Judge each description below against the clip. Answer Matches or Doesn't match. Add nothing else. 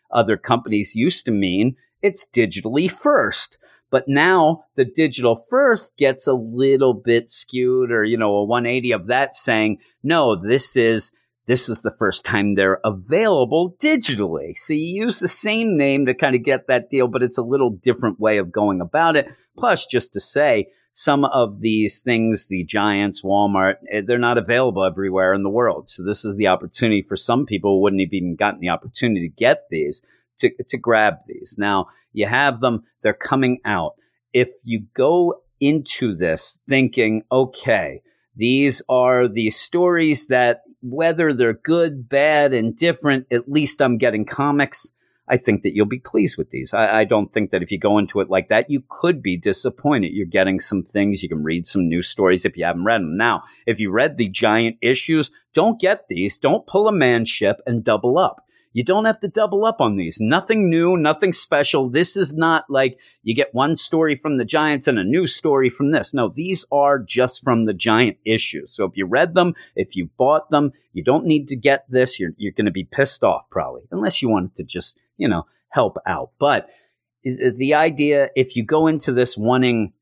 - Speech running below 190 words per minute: Doesn't match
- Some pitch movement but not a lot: Doesn't match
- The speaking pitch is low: Matches